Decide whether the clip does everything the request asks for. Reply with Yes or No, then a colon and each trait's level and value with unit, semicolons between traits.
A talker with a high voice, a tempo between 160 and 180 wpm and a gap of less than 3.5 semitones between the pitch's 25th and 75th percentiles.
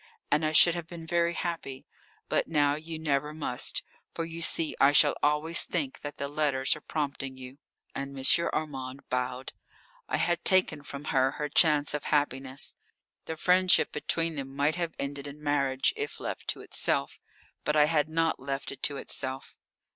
No: medium, 150 Hz; average, 175 wpm; average, 2.8 semitones